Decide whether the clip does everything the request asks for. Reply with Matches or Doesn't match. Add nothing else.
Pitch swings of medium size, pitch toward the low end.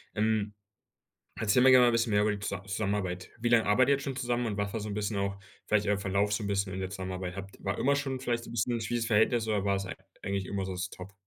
Matches